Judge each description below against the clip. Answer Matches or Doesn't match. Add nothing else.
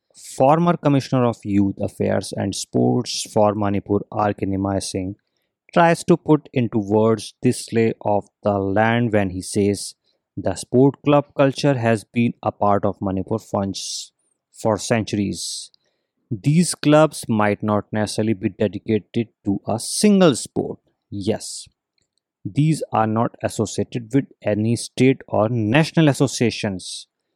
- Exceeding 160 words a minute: Doesn't match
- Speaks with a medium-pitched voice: Doesn't match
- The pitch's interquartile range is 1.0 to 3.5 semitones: Doesn't match